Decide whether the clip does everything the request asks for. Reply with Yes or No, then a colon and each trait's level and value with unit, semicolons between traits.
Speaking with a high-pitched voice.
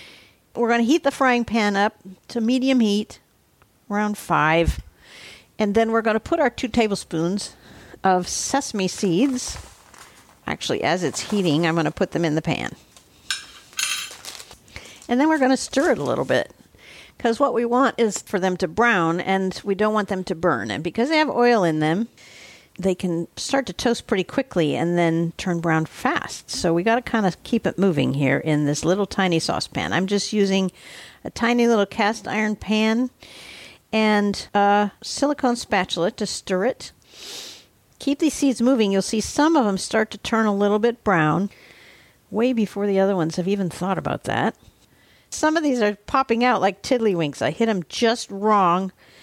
Yes: high, 205 Hz